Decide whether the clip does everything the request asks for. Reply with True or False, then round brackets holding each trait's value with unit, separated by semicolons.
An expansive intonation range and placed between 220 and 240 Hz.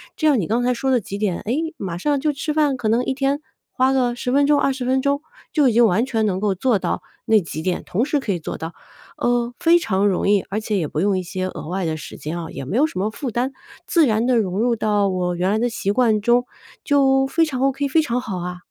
True (5.8 semitones; 235 Hz)